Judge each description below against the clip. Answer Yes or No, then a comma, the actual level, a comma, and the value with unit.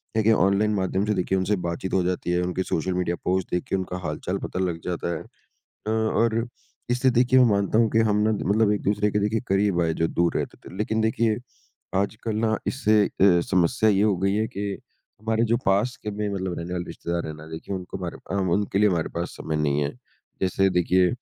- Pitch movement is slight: No, average, 3.2 semitones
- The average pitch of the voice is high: No, low, 100 Hz